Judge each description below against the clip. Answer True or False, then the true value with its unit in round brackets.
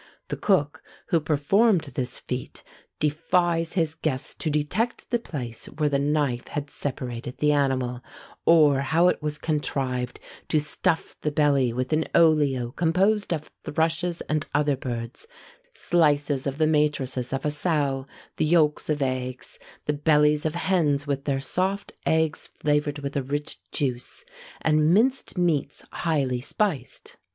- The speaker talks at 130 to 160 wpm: True (145 wpm)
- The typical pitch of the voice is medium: True (150 Hz)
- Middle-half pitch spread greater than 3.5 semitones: False (2.9 semitones)